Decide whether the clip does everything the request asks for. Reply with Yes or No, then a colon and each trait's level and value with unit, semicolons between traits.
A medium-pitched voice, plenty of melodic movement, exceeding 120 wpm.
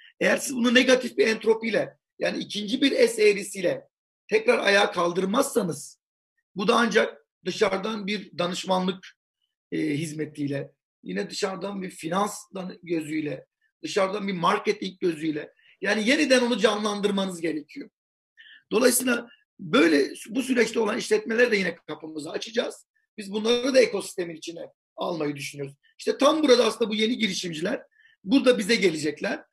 No: high, 210 Hz; wide, 5.7 semitones; average, 130 wpm